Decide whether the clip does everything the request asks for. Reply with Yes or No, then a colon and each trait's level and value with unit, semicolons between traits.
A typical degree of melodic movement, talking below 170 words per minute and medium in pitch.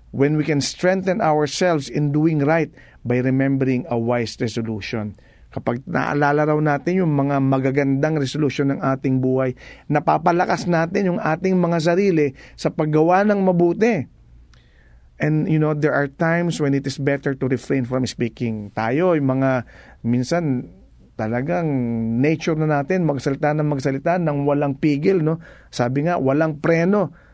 Yes: average, 4.0 semitones; average, 145 wpm; medium, 145 Hz